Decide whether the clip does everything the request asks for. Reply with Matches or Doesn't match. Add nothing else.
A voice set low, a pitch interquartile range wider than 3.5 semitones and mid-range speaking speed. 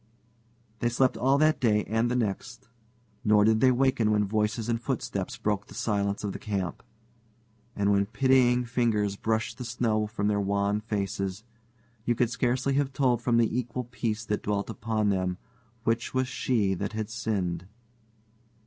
Doesn't match